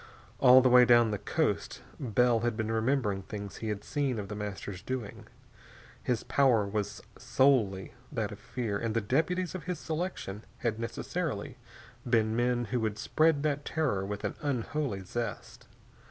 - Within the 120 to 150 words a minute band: No, average, 165 wpm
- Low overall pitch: Yes, low, 115 Hz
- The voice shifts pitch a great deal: No, average, 4.3 semitones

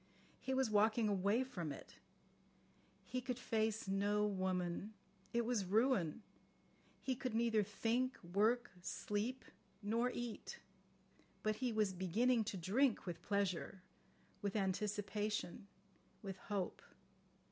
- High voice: Yes, high, 210 Hz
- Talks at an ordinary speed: No, slow, 115 wpm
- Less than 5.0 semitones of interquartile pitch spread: Yes, average, 3.3 semitones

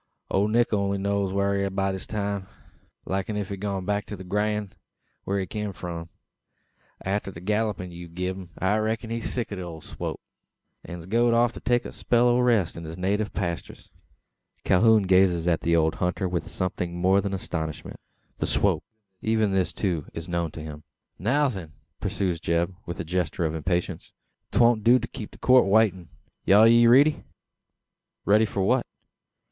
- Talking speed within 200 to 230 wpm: No, average, 185 wpm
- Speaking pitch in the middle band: No, very low, 95 Hz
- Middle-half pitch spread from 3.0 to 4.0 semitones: Yes, average, 3.4 semitones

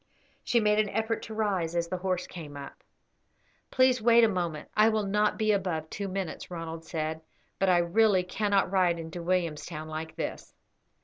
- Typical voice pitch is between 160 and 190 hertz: Yes, medium, 185 Hz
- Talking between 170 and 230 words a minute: Yes, average, 180 wpm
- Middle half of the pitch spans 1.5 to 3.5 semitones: No, average, 4.2 semitones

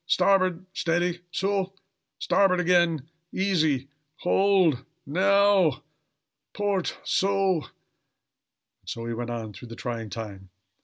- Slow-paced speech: Yes, slow, 105 wpm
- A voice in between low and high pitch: Yes, medium, 175 Hz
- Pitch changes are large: Yes, wide, 7.3 semitones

